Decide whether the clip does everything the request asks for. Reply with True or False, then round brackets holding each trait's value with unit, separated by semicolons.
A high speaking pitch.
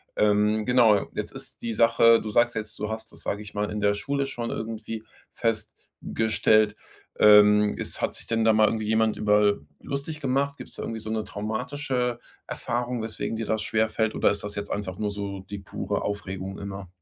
False (110 Hz)